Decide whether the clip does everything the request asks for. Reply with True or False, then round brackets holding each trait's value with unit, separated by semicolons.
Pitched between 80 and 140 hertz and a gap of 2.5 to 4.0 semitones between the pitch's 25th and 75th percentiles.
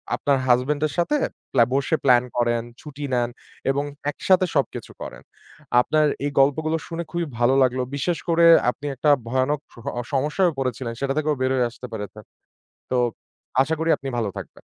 True (135 Hz; 3.6 semitones)